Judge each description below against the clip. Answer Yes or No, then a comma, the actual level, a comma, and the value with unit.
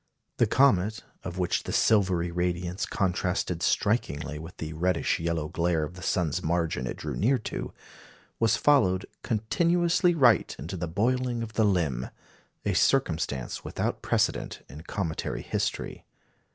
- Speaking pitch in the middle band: No, very low, 90 Hz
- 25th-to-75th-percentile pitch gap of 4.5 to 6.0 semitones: Yes, average, 5.1 semitones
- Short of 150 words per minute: Yes, average, 140 wpm